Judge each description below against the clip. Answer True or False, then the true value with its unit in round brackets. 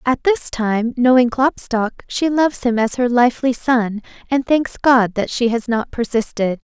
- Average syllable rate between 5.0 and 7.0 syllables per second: False (4.4 syllables/s)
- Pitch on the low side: False (245 Hz)